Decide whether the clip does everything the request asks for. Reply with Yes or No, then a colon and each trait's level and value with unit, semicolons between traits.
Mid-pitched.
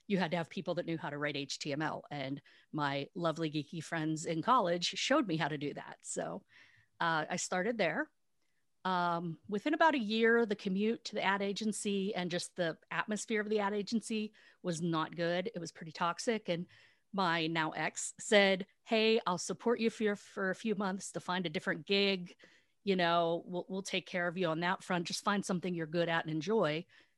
Yes: medium, 180 Hz